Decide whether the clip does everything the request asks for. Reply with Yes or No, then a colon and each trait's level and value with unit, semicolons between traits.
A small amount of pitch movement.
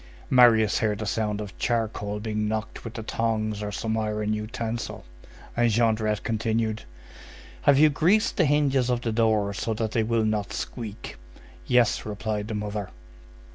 Yes: narrow, 1.7 semitones